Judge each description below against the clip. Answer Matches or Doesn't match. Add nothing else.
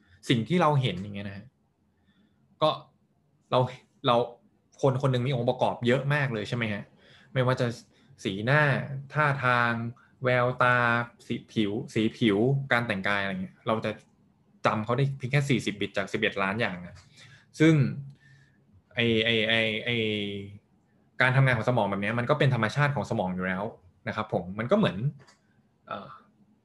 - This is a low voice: Matches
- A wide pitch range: Doesn't match